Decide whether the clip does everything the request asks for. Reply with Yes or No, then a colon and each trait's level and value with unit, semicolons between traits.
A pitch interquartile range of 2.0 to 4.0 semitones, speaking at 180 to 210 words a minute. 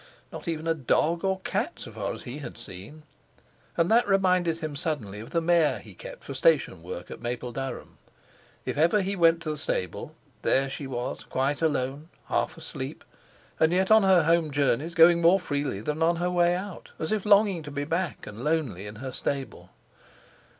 No: average, 4.5 semitones; average, 190 wpm